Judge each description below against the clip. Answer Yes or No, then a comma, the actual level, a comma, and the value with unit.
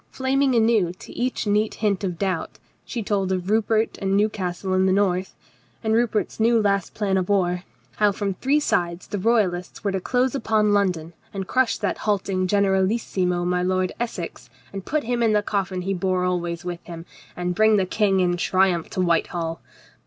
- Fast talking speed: No, average, 185 wpm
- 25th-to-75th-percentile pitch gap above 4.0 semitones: No, average, 3.2 semitones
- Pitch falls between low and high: No, high, 195 Hz